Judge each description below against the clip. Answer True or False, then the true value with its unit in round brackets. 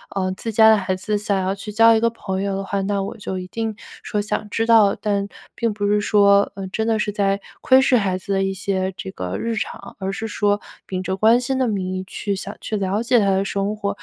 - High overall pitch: True (200 Hz)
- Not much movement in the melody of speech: True (2.2 semitones)